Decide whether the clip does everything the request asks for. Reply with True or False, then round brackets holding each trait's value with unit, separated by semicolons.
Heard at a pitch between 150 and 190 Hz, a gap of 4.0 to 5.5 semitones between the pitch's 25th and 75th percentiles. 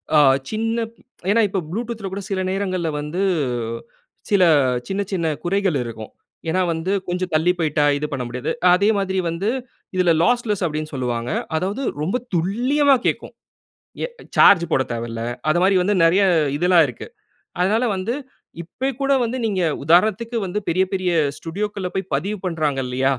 True (185 Hz; 4.5 semitones)